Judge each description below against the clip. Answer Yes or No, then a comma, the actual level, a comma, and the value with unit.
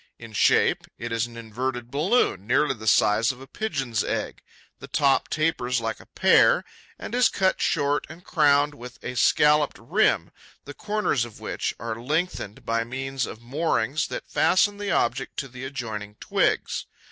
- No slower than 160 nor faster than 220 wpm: Yes, average, 170 wpm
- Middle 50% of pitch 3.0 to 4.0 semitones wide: No, average, 4.5 semitones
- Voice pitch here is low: Yes, low, 130 Hz